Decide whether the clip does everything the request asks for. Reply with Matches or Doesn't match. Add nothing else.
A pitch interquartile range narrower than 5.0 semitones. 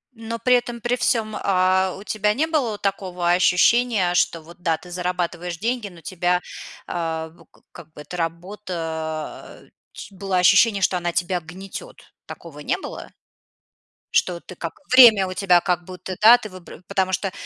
Matches